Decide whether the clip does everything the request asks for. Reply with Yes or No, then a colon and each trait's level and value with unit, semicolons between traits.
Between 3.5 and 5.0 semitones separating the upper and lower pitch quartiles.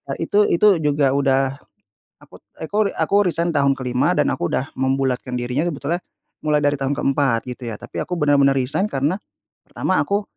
Yes: average, 3.8 semitones